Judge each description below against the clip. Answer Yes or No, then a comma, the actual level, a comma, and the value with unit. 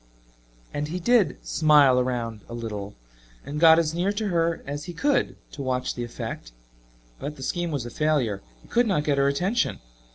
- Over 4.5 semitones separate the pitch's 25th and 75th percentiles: Yes, average, 5.2 semitones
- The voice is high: No, medium, 150 Hz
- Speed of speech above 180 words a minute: Yes, average, 190 wpm